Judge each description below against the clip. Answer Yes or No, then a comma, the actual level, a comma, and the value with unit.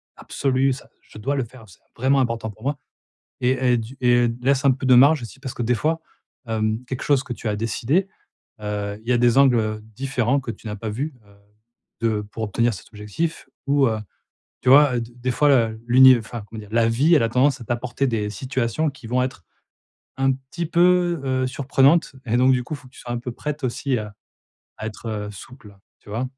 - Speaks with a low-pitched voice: Yes, low, 125 Hz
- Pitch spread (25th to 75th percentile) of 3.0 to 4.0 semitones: Yes, average, 3.3 semitones